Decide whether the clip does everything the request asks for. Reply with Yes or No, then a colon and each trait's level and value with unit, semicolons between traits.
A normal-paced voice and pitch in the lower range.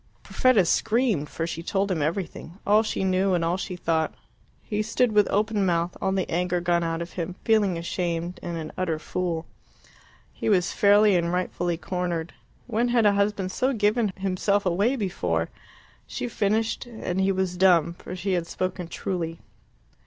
No: average, 175 wpm; medium, 185 Hz